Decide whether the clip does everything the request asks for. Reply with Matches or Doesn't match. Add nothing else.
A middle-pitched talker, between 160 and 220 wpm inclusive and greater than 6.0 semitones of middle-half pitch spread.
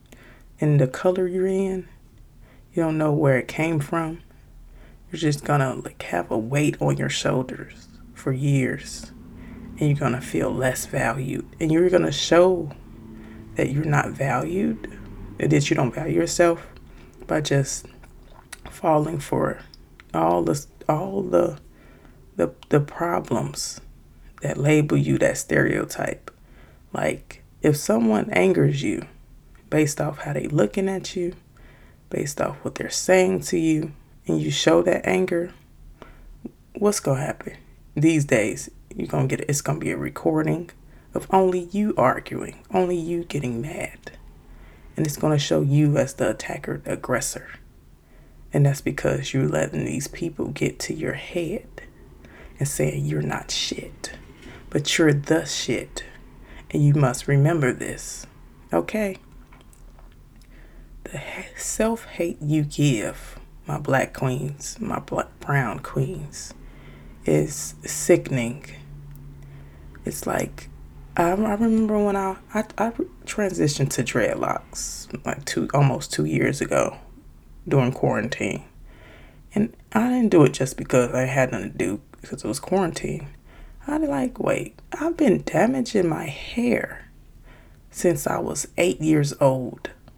Doesn't match